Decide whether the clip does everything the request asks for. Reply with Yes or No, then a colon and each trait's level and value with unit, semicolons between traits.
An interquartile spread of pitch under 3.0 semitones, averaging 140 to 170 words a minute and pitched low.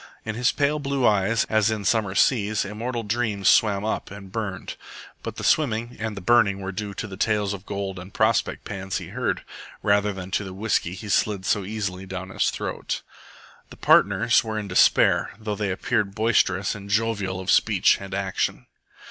No: narrow, 2.4 semitones; average, 190 wpm; low, 105 Hz